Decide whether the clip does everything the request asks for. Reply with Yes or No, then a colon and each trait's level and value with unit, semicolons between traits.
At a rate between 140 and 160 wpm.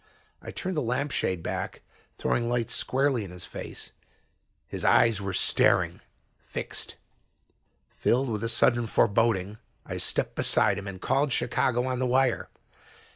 Yes: average, 145 wpm